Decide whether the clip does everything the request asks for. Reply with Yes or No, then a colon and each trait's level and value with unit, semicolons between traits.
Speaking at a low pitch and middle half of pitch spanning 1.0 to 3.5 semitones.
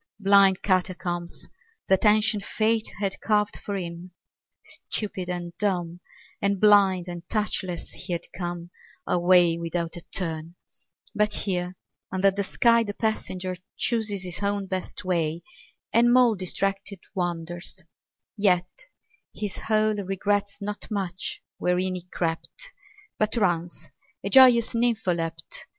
No: high, 190 Hz; average, 2.9 semitones